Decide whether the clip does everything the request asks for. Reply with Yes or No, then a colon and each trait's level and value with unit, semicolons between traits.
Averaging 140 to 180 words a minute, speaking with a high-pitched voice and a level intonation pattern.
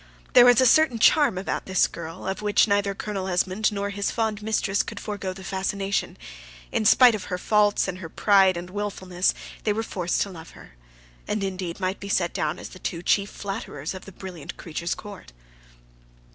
No: average, 195 wpm; high, 195 Hz; narrow, 2.1 semitones